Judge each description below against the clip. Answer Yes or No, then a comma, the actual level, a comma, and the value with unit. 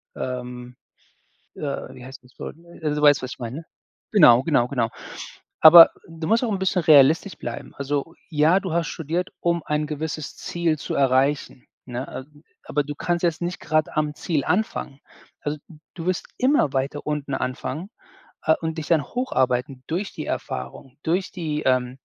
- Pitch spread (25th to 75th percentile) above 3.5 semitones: Yes, average, 4.1 semitones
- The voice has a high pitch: No, medium, 150 Hz